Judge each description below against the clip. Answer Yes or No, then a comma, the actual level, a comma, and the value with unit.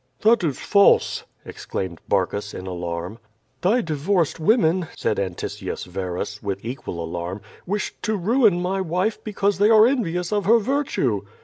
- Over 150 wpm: No, average, 145 wpm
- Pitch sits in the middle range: Yes, medium, 170 Hz